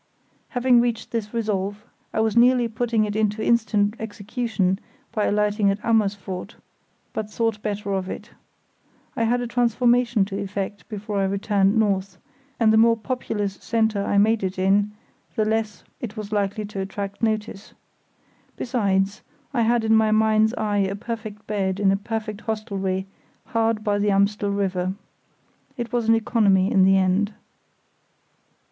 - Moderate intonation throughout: No, narrow, 2.2 semitones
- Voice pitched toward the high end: Yes, high, 210 Hz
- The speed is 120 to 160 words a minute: Yes, average, 155 wpm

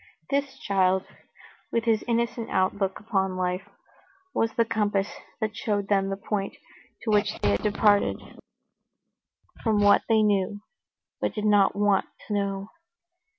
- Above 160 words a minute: No, average, 140 wpm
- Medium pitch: No, high, 205 Hz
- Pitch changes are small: Yes, narrow, 1.9 semitones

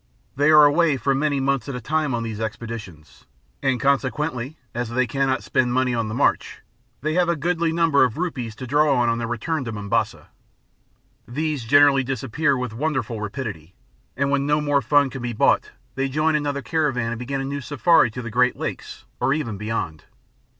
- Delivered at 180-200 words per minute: Yes, average, 190 wpm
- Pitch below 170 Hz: Yes, low, 135 Hz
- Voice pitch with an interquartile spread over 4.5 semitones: No, average, 3.8 semitones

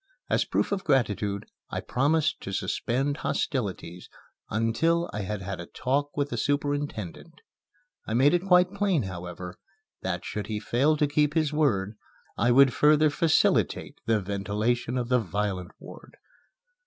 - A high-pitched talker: No, low, 120 Hz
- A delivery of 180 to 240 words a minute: No, average, 150 wpm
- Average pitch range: No, wide, 6.5 semitones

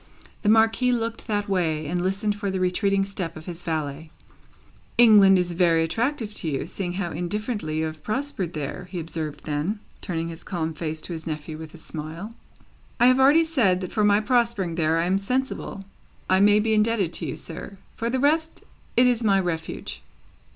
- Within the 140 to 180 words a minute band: No, average, 195 wpm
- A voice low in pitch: No, high, 190 Hz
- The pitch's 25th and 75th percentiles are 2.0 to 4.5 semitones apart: No, average, 5.2 semitones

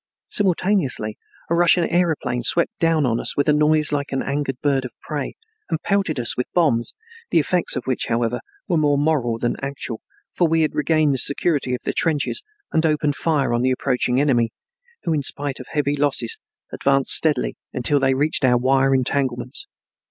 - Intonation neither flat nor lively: Yes, average, 3.5 semitones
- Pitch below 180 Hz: Yes, medium, 140 Hz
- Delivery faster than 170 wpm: Yes, average, 185 wpm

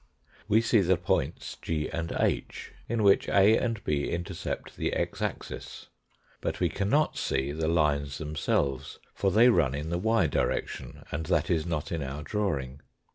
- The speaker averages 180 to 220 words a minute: No, average, 170 wpm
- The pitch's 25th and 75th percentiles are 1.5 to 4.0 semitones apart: No, wide, 5.4 semitones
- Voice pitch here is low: Yes, very low, 80 Hz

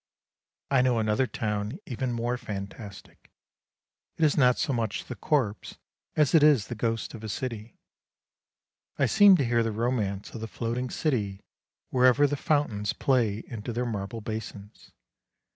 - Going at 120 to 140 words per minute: No, average, 155 wpm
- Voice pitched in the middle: No, low, 115 Hz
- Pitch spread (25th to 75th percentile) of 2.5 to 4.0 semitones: Yes, average, 3.3 semitones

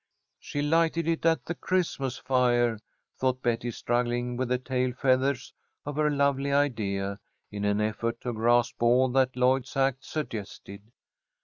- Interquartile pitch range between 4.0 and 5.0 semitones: No, average, 2.8 semitones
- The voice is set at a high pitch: No, low, 125 Hz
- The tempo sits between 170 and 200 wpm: No, average, 145 wpm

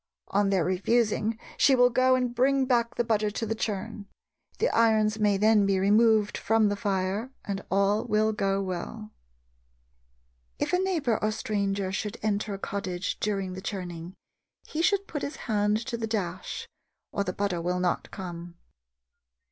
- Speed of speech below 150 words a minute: No, average, 165 wpm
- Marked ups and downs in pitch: No, average, 2.7 semitones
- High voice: Yes, high, 210 Hz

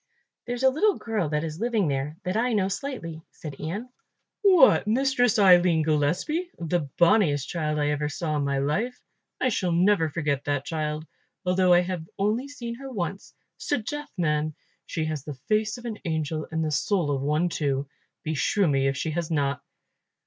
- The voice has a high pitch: No, medium, 170 Hz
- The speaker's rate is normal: Yes, average, 180 wpm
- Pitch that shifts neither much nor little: No, wide, 6.2 semitones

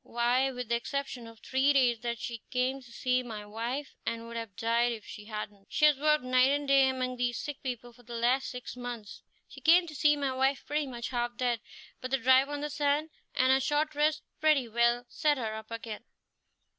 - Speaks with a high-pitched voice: Yes, very high, 250 Hz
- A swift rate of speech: Yes, fast, 220 wpm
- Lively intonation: No, average, 2.9 semitones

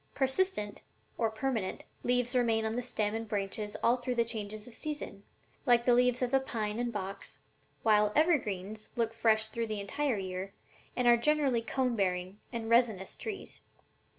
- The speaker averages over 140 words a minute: Yes, average, 170 wpm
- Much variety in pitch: No, average, 2.9 semitones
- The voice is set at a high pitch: Yes, high, 230 Hz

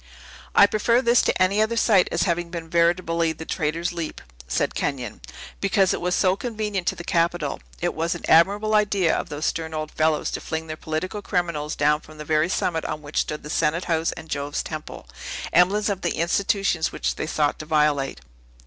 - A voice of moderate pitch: Yes, medium, 170 Hz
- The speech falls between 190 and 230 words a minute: Yes, average, 200 wpm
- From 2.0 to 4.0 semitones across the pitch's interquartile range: Yes, average, 3.5 semitones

